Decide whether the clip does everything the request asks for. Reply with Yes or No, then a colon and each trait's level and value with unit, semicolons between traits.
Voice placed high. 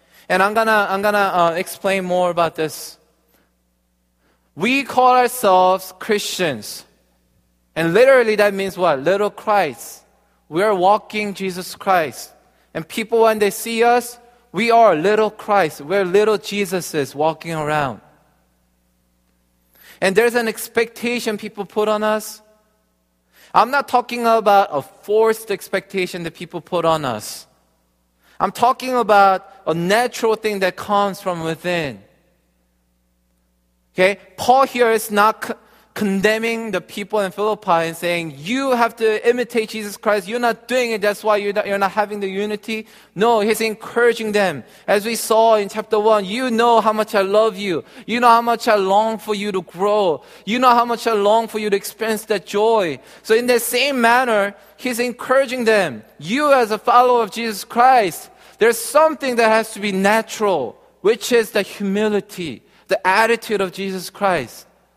Yes: high, 210 Hz